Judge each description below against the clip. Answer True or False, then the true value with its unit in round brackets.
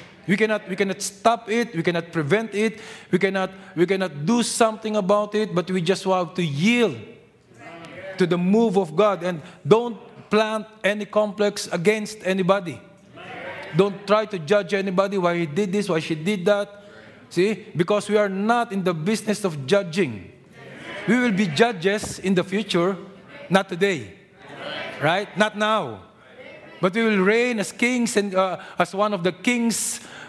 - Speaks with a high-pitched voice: True (200 Hz)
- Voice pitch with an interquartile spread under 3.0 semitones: True (2.5 semitones)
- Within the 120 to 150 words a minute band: False (165 wpm)